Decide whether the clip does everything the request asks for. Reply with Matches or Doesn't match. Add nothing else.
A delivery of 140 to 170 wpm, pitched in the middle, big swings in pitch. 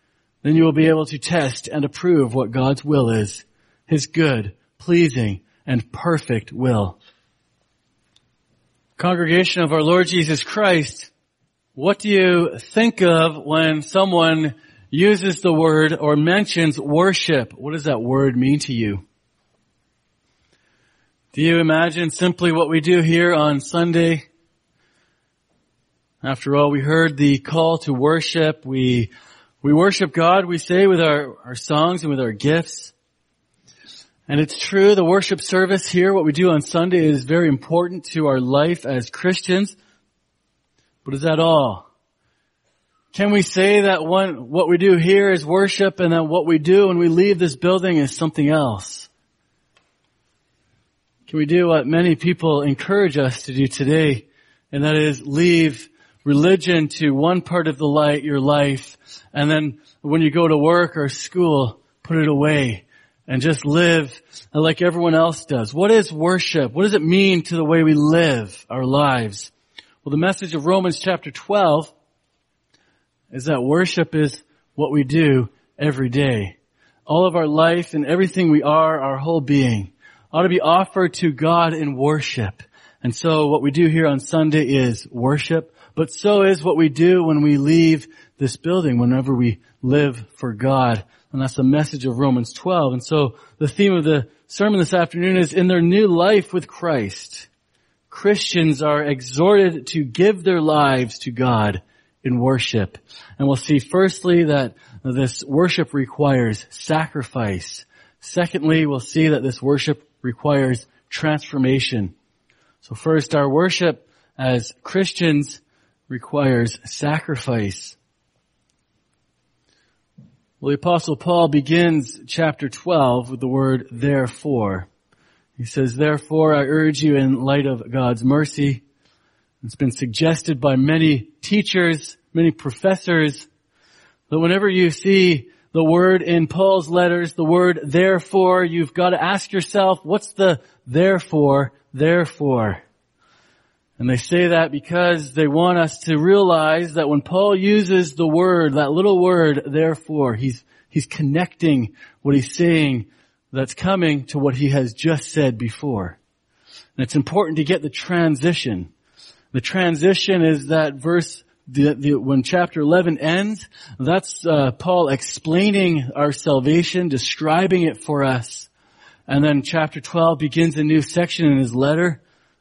Doesn't match